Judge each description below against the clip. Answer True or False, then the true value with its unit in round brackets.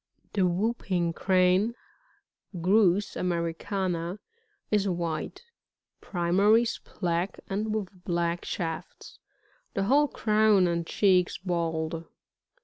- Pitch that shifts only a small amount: False (3.3 semitones)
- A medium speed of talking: False (105 wpm)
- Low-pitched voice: False (185 Hz)